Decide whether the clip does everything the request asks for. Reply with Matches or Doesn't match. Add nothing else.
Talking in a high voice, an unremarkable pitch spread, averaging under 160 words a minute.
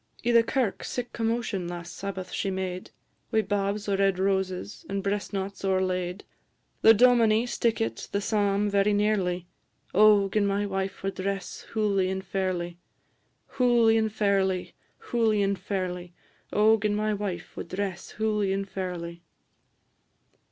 Doesn't match